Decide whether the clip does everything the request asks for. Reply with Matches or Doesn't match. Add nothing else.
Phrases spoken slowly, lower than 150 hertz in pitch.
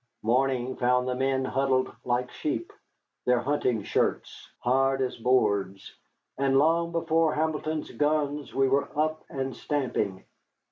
Matches